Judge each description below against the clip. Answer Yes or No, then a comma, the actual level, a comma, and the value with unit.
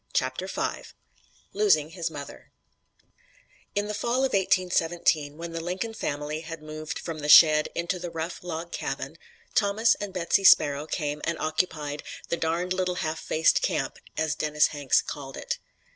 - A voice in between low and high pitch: Yes, medium, 165 Hz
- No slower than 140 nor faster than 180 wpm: Yes, average, 160 wpm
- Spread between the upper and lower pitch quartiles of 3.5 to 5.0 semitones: No, average, 3.0 semitones